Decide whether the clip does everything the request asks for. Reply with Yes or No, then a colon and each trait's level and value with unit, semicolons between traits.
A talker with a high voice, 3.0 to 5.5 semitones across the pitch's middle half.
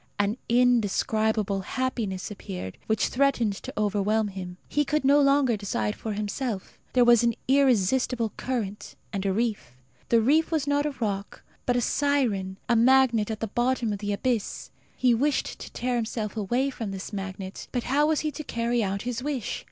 Yes: high, 230 Hz; average, 4.2 semitones